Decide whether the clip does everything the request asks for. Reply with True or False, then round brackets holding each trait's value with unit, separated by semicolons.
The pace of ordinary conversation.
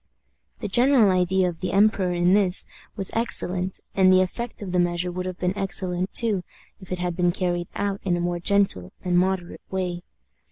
True (195 wpm)